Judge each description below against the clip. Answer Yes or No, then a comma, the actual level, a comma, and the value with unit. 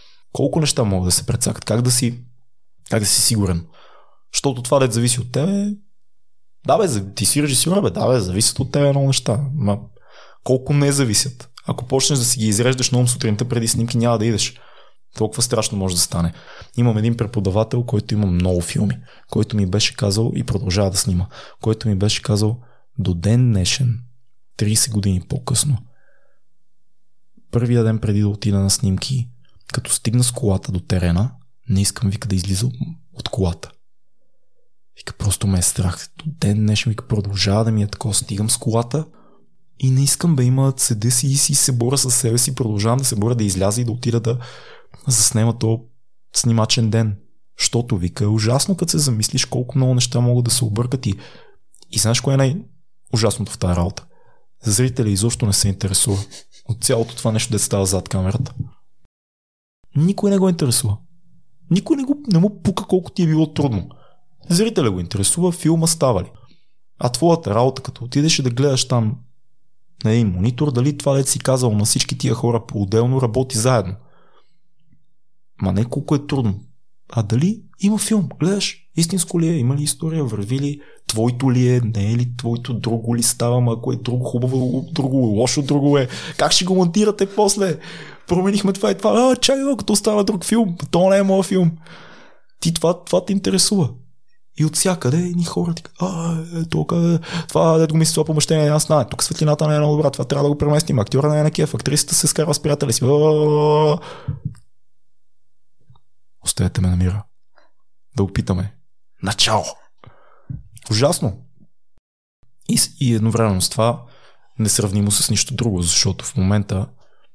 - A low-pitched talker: Yes, low, 125 Hz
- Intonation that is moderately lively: No, wide, 5.7 semitones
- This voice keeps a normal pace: No, fast, 175 wpm